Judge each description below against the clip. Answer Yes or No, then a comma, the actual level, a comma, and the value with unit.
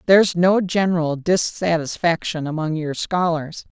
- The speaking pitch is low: No, medium, 170 Hz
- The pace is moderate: No, slow, 110 wpm